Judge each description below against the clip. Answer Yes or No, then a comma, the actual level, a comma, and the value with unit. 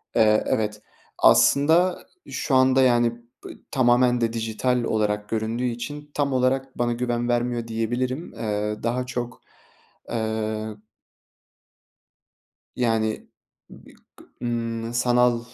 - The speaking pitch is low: Yes, low, 120 Hz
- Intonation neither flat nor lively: No, narrow, 2.1 semitones